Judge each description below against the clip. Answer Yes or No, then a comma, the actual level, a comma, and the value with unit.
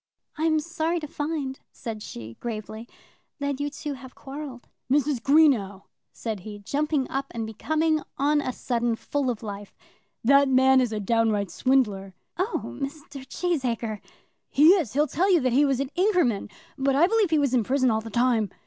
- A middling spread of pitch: Yes, average, 4.7 semitones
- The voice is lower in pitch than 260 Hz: No, very high, 265 Hz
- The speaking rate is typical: Yes, average, 175 wpm